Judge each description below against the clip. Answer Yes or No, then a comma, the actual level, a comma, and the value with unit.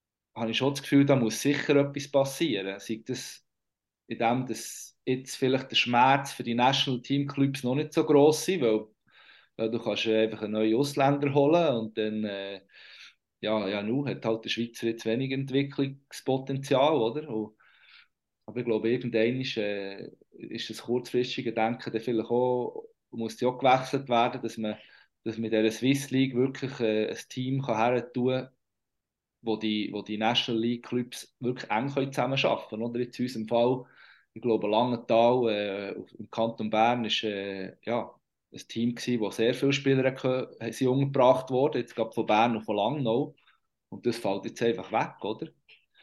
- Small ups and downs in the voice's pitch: No, average, 3.1 semitones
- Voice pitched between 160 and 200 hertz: No, low, 120 Hz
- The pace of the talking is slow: No, average, 170 wpm